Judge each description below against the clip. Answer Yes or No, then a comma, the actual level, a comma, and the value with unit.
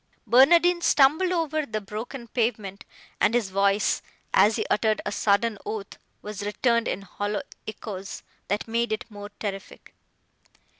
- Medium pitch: No, high, 215 Hz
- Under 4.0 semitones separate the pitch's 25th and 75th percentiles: Yes, average, 3.0 semitones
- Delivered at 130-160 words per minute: Yes, average, 140 wpm